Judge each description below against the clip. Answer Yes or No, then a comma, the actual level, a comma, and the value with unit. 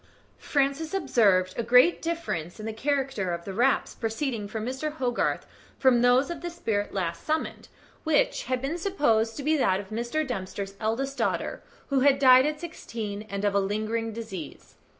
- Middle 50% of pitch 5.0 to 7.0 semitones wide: Yes, wide, 5.6 semitones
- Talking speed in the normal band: Yes, average, 175 wpm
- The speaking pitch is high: Yes, high, 245 Hz